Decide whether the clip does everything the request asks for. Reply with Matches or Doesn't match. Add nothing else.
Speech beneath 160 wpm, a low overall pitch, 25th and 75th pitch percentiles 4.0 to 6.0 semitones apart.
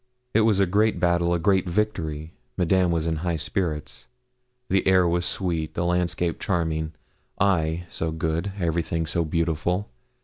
Doesn't match